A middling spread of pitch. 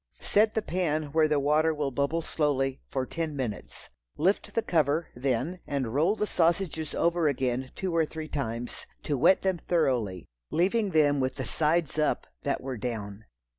Yes: average, 4.0 semitones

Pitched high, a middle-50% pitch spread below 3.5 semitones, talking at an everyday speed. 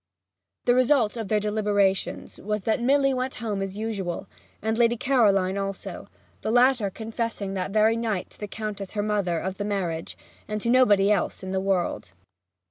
Yes: high, 210 Hz; average, 2.8 semitones; average, 175 wpm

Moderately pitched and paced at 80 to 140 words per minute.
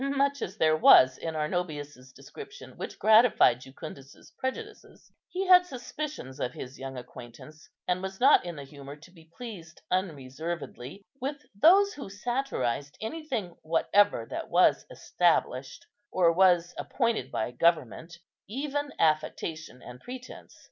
Yes: medium, 175 Hz; slow, 135 wpm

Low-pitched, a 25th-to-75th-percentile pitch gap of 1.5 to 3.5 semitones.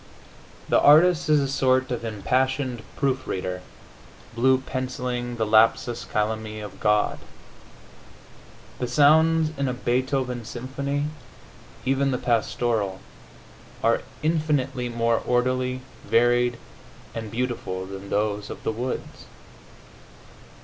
Yes: low, 125 Hz; average, 2.9 semitones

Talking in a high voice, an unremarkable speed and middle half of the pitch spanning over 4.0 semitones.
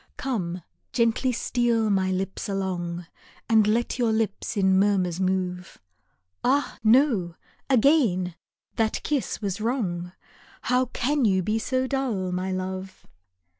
No: high, 205 Hz; slow, 125 wpm; average, 4.4 semitones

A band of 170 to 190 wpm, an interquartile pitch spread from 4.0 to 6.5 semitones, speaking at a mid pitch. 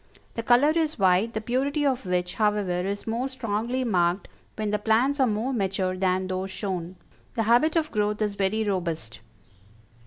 No: average, 175 wpm; average, 4.6 semitones; high, 210 Hz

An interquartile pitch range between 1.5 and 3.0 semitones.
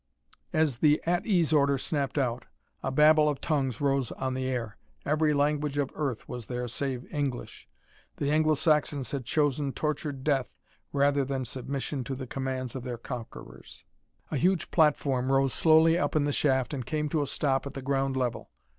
Yes: narrow, 2.4 semitones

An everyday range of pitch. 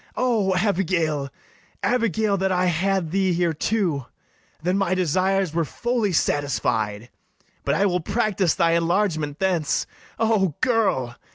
Yes: average, 3.9 semitones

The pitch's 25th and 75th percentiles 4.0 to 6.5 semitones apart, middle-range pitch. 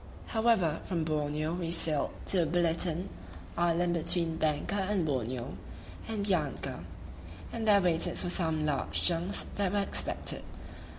No: average, 3.3 semitones; medium, 170 Hz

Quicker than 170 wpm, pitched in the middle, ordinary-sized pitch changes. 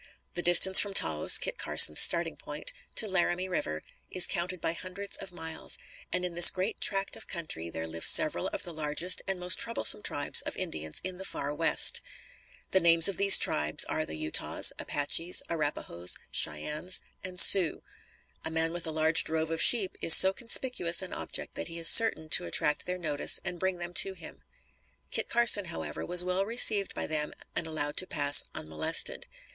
Yes: average, 185 wpm; medium, 175 Hz; average, 3.6 semitones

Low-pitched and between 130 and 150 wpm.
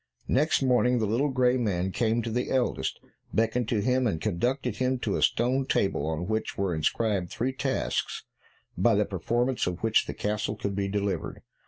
No: low, 115 Hz; average, 185 wpm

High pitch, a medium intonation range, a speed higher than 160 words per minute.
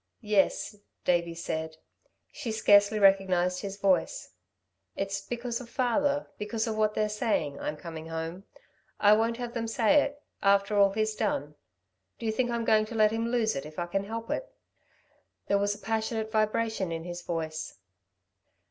Yes: high, 210 Hz; average, 3.8 semitones; average, 170 wpm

